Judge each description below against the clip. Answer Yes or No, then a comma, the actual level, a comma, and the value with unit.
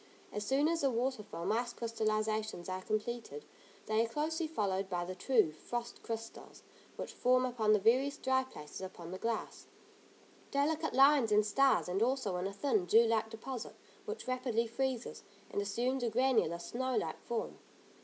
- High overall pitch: Yes, high, 230 Hz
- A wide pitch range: No, average, 3.8 semitones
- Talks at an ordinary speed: Yes, average, 170 wpm